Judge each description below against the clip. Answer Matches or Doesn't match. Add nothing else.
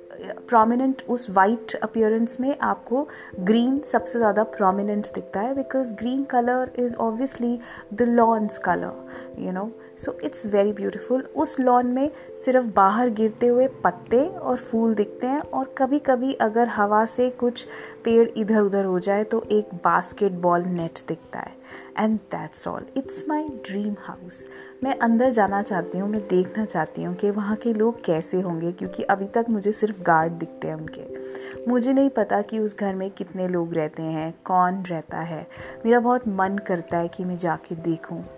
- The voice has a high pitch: Matches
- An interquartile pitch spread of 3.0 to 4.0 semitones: Doesn't match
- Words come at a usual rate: Matches